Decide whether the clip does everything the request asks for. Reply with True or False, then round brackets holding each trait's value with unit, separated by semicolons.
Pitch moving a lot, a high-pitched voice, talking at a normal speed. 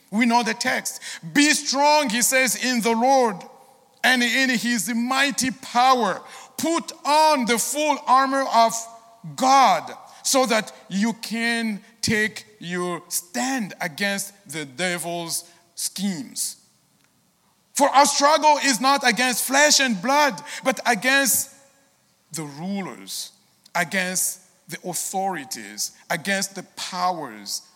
False (6.2 semitones; 235 Hz; 115 wpm)